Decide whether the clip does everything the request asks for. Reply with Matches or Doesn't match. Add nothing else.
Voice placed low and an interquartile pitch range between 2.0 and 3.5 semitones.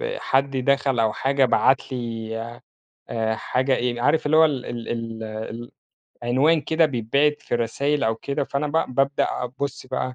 Matches